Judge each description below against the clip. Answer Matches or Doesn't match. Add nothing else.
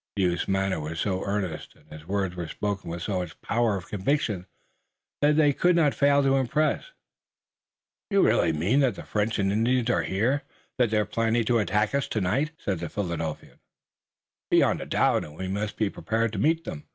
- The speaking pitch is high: Doesn't match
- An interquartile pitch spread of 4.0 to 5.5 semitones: Matches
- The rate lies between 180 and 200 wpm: Matches